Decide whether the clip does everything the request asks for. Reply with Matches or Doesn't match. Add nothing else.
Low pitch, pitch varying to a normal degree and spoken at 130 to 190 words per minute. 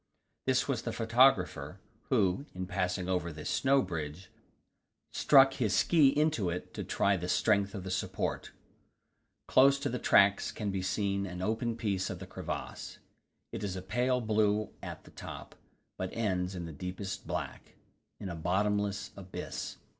Matches